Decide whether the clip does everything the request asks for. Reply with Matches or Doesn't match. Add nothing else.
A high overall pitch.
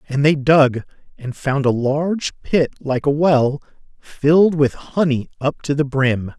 Doesn't match